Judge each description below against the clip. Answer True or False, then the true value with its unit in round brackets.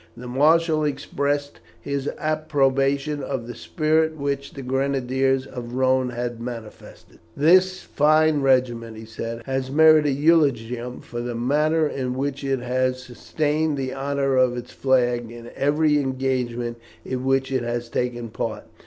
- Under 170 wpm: True (150 wpm)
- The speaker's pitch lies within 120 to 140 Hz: True (135 Hz)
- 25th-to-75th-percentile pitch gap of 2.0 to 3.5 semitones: True (2.9 semitones)